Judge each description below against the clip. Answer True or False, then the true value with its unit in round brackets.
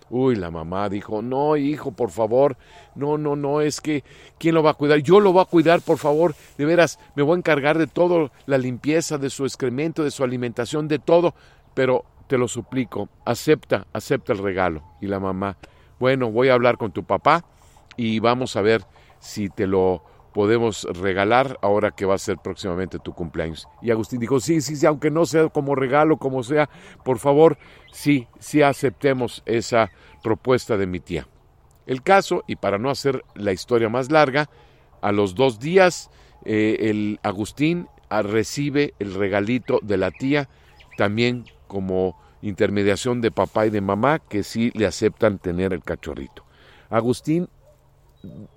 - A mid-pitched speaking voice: False (125 Hz)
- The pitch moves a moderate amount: False (6.5 semitones)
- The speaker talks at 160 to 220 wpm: True (175 wpm)